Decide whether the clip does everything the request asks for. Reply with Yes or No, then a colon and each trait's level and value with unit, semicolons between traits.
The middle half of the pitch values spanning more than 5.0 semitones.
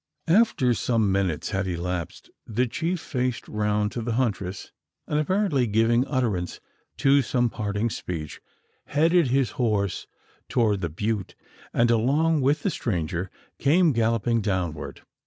Yes: wide, 5.4 semitones